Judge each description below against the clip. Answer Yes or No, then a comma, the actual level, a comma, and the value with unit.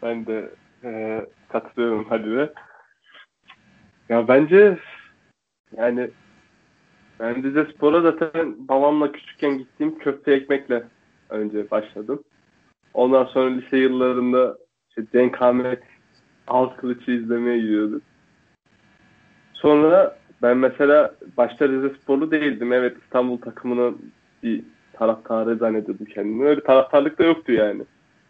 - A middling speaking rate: Yes, average, 105 wpm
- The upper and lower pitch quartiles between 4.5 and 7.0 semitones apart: No, average, 3.7 semitones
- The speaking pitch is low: Yes, low, 125 Hz